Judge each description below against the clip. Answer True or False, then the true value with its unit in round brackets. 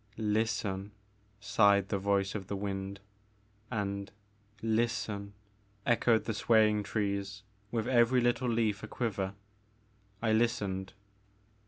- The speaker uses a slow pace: True (110 wpm)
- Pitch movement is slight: True (2.3 semitones)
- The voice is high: False (105 Hz)